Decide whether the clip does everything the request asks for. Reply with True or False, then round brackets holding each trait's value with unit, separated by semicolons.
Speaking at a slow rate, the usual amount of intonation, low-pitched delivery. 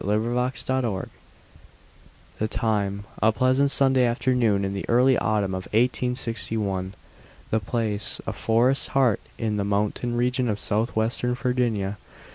True (130 wpm; 3.2 semitones; 115 Hz)